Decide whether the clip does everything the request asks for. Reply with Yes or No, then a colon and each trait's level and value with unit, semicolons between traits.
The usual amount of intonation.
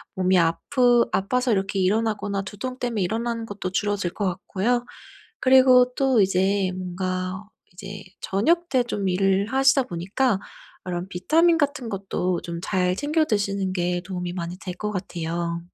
Yes: average, 4.9 semitones